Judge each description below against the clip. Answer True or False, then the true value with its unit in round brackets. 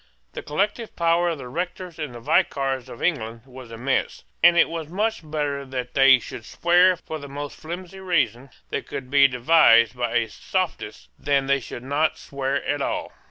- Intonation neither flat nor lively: True (4.8 semitones)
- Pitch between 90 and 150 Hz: True (140 Hz)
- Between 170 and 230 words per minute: True (180 wpm)